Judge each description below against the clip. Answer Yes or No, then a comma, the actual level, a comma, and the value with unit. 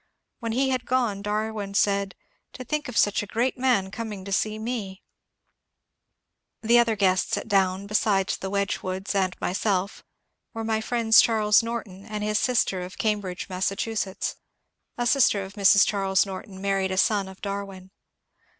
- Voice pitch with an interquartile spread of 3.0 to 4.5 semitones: No, narrow, 2.6 semitones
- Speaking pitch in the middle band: No, high, 205 Hz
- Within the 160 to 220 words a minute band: Yes, average, 170 wpm